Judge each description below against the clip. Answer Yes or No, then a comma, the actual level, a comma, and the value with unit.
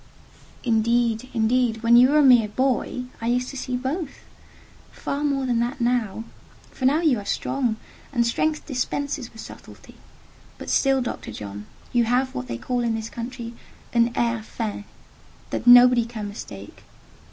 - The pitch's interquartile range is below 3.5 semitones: Yes, narrow, 2.4 semitones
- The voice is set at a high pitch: Yes, high, 240 Hz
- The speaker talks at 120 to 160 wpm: Yes, average, 150 wpm